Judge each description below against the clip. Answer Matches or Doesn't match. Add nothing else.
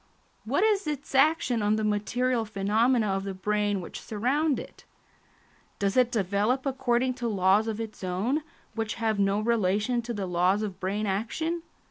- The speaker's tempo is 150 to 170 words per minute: Matches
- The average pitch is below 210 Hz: Doesn't match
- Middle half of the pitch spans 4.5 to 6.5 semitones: Doesn't match